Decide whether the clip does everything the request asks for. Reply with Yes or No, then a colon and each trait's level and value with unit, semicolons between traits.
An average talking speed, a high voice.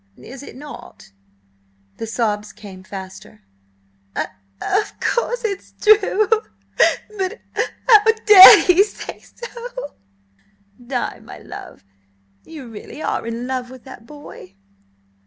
No: slow, 115 wpm; very high, 265 Hz